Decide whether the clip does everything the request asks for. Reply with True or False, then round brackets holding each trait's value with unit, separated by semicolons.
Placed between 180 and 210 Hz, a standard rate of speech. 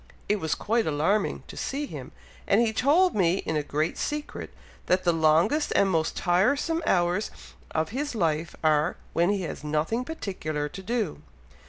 True (185 Hz; 170 wpm)